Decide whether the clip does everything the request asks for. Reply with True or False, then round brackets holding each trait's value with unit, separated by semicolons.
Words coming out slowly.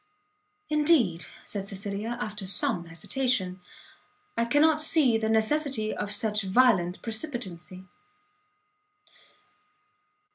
True (85 wpm)